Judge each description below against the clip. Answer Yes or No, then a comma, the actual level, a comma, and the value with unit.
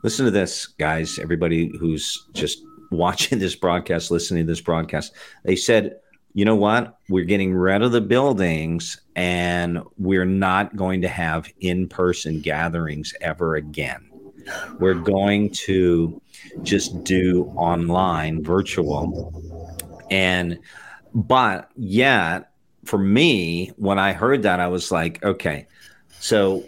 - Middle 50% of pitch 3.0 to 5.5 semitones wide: No, narrow, 2.6 semitones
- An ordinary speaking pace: No, slow, 130 wpm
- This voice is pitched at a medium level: No, very low, 90 Hz